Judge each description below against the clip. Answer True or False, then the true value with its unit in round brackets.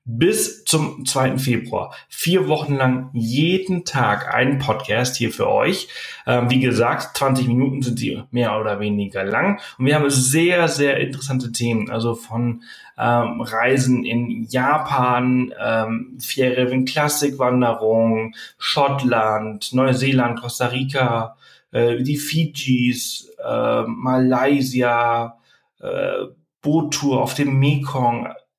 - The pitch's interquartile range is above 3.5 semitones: False (2.8 semitones)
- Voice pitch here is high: False (125 Hz)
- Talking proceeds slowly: True (120 wpm)